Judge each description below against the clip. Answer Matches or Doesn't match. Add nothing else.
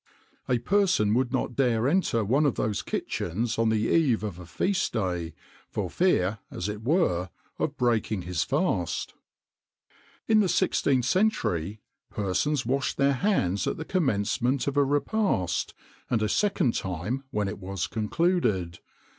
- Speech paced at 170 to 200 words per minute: Doesn't match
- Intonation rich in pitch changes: Matches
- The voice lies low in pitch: Matches